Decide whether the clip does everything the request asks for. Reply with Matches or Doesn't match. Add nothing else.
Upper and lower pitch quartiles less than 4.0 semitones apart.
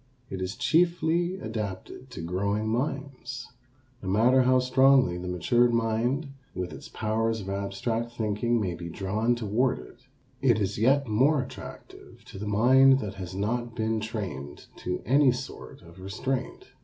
Doesn't match